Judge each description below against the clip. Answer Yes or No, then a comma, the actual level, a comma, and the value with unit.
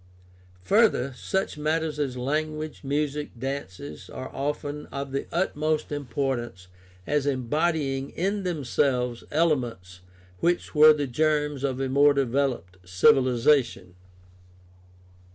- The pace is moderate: No, slow, 110 wpm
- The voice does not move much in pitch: No, average, 3.3 semitones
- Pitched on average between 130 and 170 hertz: Yes, medium, 140 Hz